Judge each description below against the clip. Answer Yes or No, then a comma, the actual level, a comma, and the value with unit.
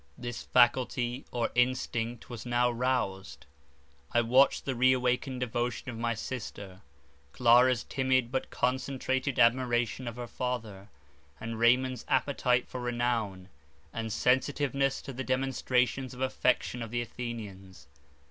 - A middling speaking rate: No, slow, 130 wpm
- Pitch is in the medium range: No, low, 125 Hz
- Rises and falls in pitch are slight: Yes, narrow, 1.8 semitones